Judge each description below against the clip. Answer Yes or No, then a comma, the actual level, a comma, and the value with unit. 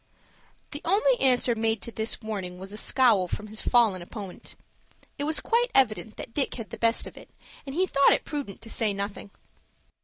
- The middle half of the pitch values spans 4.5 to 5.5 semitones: Yes, average, 4.8 semitones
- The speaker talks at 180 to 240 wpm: Yes, average, 195 wpm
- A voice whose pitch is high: Yes, high, 225 Hz